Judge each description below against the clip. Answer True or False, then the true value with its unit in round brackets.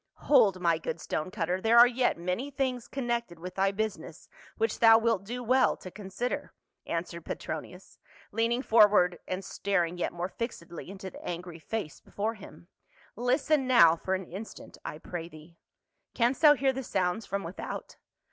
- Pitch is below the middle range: False (195 Hz)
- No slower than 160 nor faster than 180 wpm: True (175 wpm)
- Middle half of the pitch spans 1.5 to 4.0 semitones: False (5.2 semitones)